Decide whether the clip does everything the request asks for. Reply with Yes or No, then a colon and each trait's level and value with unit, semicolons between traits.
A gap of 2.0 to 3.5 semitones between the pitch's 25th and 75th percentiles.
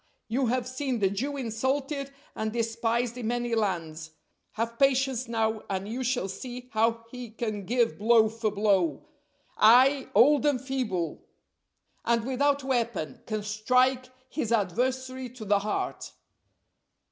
Yes: average, 3.1 semitones